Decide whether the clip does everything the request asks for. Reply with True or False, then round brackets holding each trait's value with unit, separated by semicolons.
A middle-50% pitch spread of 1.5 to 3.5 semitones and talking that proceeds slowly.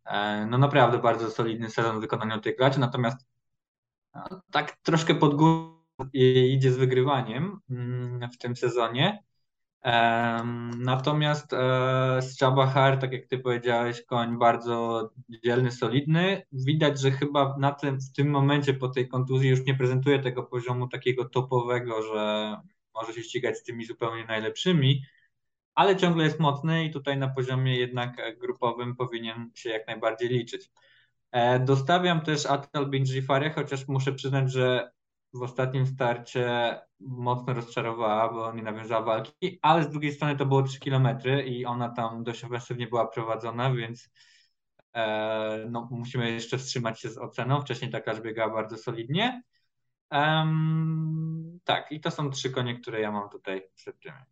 False (2.9 semitones; 140 wpm)